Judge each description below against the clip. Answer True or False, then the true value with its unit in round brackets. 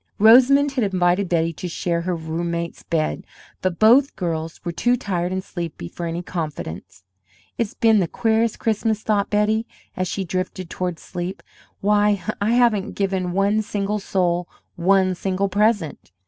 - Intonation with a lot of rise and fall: False (3.5 semitones)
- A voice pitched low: False (190 Hz)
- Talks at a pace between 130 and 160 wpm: True (155 wpm)